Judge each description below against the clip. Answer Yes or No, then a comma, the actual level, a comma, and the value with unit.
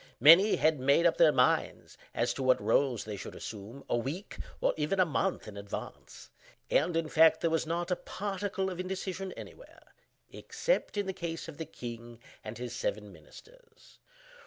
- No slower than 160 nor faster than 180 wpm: Yes, average, 175 wpm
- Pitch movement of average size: No, wide, 7.0 semitones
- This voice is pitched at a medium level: Yes, medium, 160 Hz